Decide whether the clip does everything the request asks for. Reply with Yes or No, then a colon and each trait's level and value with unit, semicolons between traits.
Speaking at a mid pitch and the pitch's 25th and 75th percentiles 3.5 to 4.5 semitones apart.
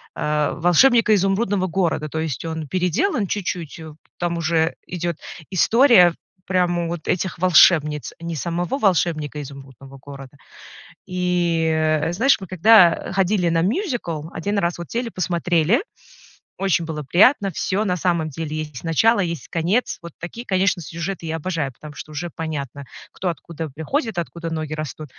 No: medium, 170 Hz; average, 3.1 semitones